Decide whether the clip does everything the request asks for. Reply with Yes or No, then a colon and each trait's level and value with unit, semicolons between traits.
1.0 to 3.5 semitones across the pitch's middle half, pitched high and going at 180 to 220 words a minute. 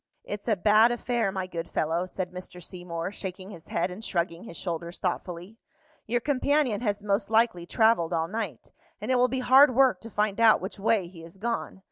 No: average, 4.4 semitones; high, 200 Hz; average, 200 wpm